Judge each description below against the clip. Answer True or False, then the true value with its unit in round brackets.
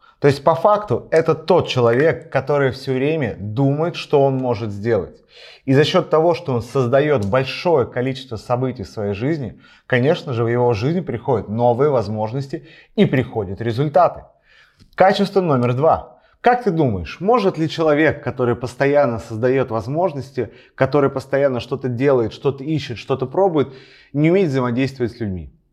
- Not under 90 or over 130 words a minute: False (150 wpm)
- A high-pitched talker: False (135 Hz)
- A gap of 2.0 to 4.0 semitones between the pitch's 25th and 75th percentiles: False (4.5 semitones)